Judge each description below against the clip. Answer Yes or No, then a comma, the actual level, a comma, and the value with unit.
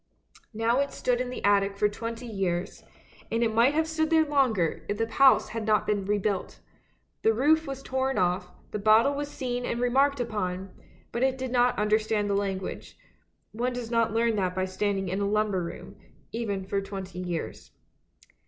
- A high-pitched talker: Yes, high, 220 Hz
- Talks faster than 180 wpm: Yes, average, 190 wpm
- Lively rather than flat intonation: No, average, 4.1 semitones